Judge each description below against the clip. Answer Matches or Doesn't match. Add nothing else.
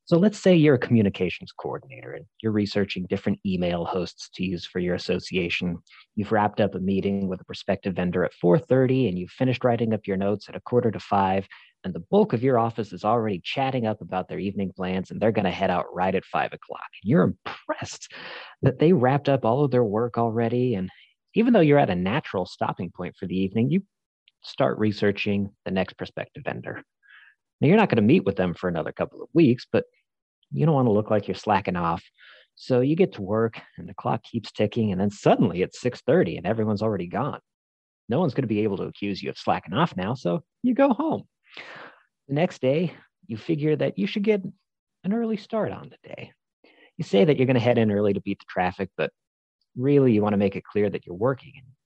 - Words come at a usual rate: Doesn't match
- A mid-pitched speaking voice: Doesn't match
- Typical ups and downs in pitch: Doesn't match